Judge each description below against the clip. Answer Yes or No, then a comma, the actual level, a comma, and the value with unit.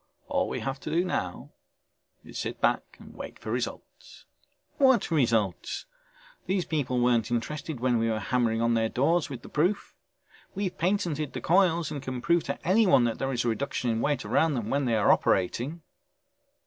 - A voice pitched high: No, low, 135 Hz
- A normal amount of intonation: No, wide, 6.1 semitones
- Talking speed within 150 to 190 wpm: Yes, average, 185 wpm